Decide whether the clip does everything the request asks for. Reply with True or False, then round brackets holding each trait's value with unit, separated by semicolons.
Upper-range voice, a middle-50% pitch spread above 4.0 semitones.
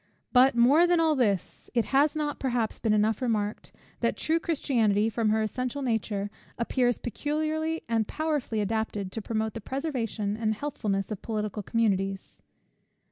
True (230 Hz; 4.6 semitones)